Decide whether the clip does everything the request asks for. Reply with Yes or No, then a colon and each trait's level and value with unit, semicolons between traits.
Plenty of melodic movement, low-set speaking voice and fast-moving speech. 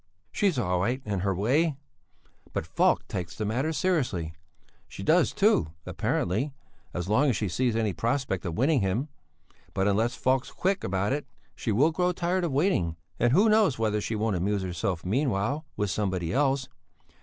No: wide, 7.0 semitones; low, 115 Hz; average, 175 wpm